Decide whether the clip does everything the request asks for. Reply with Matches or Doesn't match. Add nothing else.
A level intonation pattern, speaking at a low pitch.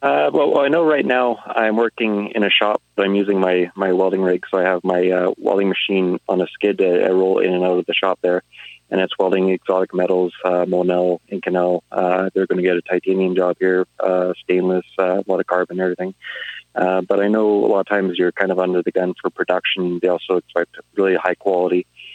Matches